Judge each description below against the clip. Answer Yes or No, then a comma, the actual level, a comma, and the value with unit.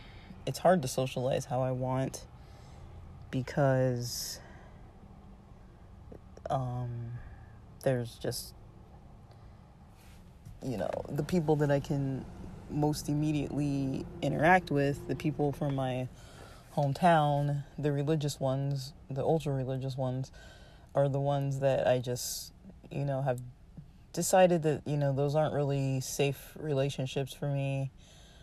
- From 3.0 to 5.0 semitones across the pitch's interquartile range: No, narrow, 2.4 semitones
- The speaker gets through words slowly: Yes, slow, 115 wpm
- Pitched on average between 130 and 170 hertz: Yes, low, 135 Hz